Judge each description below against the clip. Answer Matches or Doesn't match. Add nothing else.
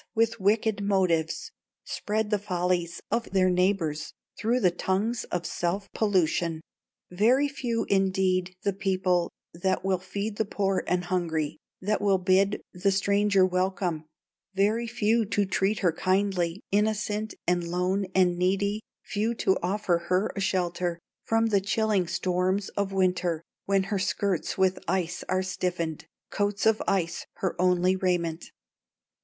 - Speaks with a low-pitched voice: Doesn't match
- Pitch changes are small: Matches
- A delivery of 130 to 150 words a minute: Matches